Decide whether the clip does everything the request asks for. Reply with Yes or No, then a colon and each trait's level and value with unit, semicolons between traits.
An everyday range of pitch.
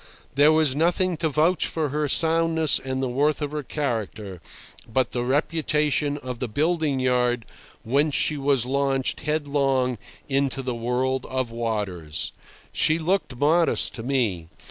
Yes: average, 3.5 semitones